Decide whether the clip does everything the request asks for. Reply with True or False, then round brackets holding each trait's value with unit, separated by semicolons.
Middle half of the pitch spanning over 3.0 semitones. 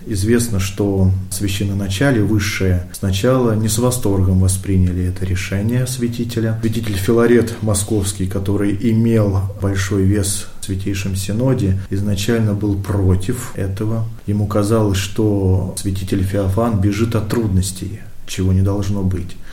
False (2.7 semitones)